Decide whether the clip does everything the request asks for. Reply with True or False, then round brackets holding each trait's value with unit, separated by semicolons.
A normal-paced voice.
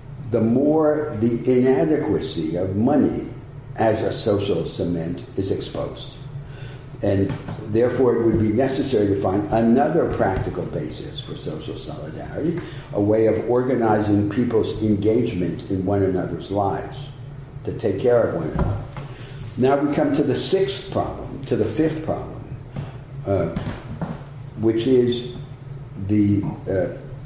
False (130 wpm)